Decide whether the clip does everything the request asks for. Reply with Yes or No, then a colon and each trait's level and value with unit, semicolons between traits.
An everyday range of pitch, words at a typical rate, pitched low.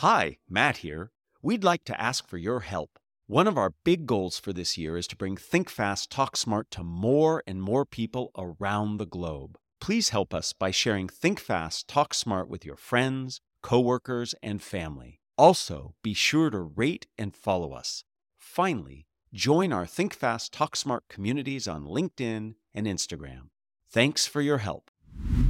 No: wide, 6.8 semitones; average, 170 wpm; low, 110 Hz